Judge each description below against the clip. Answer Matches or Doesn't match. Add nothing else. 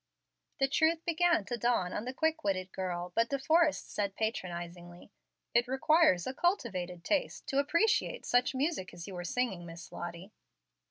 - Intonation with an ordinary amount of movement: Doesn't match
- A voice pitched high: Matches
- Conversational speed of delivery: Matches